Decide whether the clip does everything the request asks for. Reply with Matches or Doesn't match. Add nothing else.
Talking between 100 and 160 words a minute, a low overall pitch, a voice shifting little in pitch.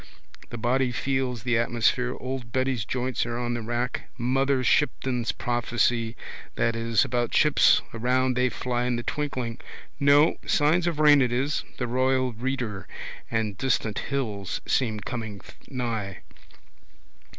Matches